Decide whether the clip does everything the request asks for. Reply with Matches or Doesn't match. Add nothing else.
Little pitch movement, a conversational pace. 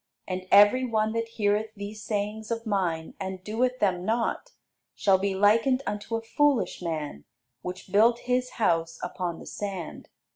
Doesn't match